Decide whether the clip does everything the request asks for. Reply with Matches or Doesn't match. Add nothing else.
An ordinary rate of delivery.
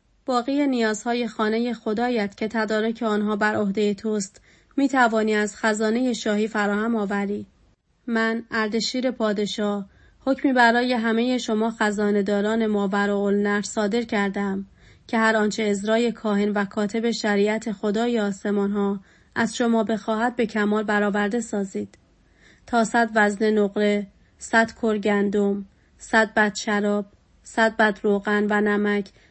Matches